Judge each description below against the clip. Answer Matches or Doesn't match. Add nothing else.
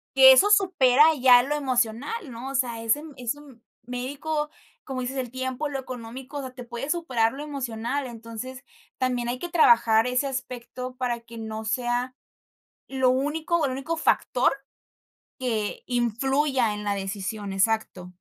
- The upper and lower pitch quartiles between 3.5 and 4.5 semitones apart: Doesn't match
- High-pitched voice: Matches